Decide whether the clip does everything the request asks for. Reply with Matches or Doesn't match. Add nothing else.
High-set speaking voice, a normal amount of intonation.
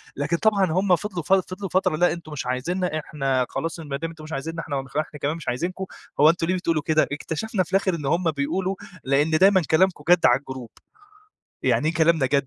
Doesn't match